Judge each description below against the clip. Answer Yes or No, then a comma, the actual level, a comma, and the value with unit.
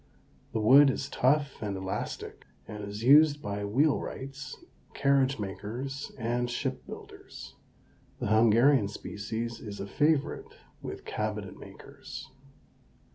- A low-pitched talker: Yes, low, 120 Hz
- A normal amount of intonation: Yes, average, 4.7 semitones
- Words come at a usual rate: No, slow, 120 wpm